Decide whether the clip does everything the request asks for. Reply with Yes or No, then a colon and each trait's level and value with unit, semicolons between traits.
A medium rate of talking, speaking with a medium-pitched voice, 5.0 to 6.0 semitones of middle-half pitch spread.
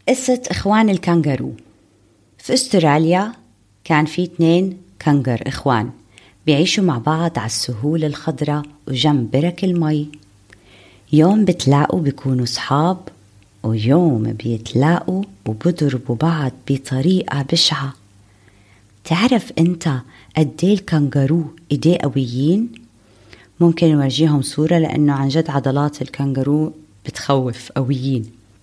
Yes: average, 95 wpm; medium, 145 Hz; wide, 5.4 semitones